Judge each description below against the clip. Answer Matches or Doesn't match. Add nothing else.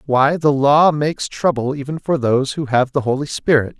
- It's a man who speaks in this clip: Matches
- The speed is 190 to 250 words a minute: Matches